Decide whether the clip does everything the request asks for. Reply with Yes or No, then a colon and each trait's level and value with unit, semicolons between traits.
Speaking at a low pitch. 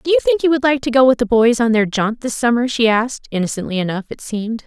No: high, 240 Hz